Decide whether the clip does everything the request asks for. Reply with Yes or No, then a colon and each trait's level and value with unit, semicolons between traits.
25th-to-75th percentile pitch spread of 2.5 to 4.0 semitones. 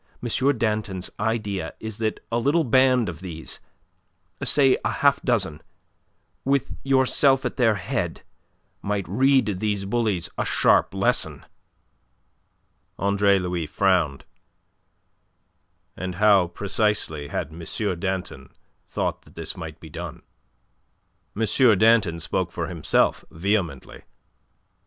No: average, 4.7 semitones